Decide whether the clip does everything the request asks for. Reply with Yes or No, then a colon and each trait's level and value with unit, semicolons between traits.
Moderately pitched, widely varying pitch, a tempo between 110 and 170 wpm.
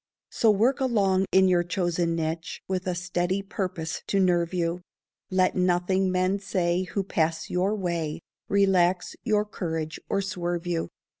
No: medium, 180 Hz; narrow, 2.0 semitones; average, 150 wpm